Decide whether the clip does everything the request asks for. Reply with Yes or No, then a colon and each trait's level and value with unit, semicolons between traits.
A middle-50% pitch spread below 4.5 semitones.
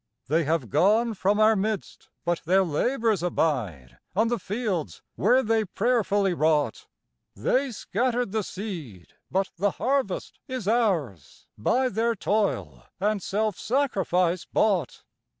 No: average, 5.2 semitones